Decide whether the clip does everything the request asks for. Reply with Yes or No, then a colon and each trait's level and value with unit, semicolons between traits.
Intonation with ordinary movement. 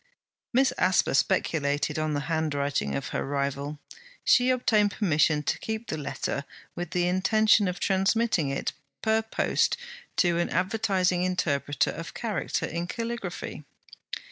No: wide, 6.4 semitones